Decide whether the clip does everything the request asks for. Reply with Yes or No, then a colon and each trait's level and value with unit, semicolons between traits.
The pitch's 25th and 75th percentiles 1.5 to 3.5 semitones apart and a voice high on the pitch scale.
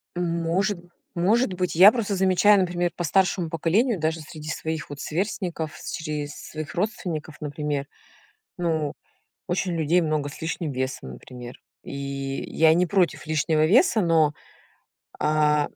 No: average, 3.1 semitones; medium, 165 Hz